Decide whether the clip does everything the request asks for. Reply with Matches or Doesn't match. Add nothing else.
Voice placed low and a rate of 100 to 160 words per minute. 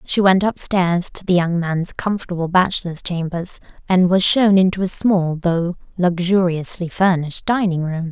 Doesn't match